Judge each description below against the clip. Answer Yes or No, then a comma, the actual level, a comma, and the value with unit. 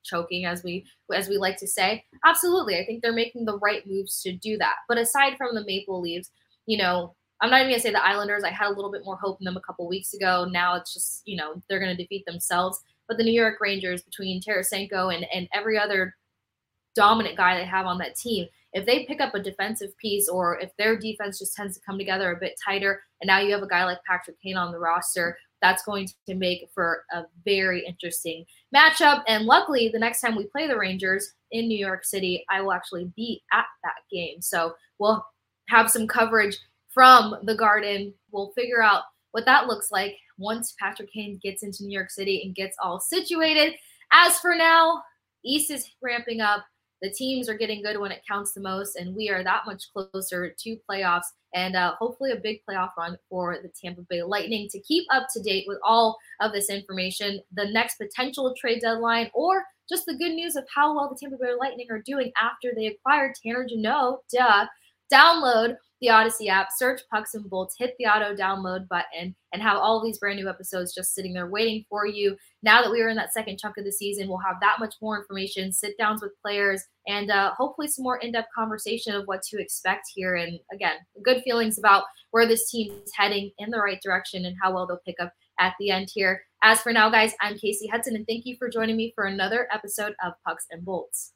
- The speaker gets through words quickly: Yes, fast, 220 wpm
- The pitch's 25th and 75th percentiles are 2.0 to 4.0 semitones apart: Yes, average, 3.4 semitones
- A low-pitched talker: No, high, 205 Hz